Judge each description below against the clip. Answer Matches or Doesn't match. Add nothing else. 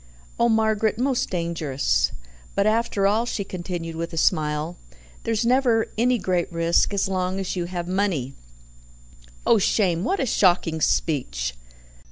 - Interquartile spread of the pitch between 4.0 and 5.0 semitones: Matches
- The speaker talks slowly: Doesn't match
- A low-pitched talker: Doesn't match